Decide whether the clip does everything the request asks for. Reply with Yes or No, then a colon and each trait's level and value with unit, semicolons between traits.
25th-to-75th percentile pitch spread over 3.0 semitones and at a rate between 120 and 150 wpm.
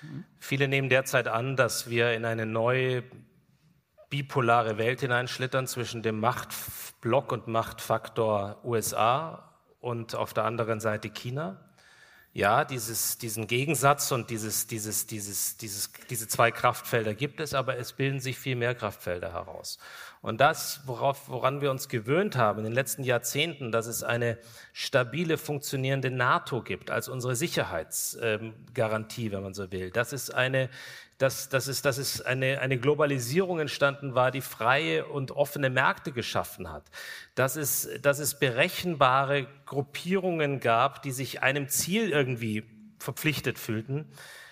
Yes: average, 3.6 semitones; average, 145 wpm